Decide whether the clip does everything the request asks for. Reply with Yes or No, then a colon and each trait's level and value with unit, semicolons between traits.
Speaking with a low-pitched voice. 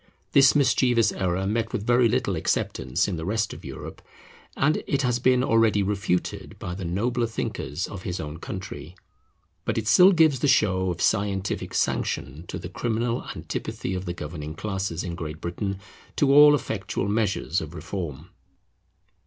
Yes: low, 100 Hz